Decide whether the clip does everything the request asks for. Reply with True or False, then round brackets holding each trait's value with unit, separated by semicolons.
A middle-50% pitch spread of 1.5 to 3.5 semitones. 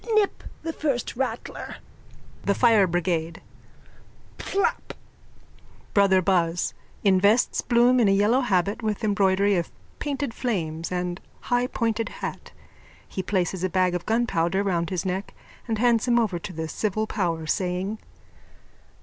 False (4.4 semitones)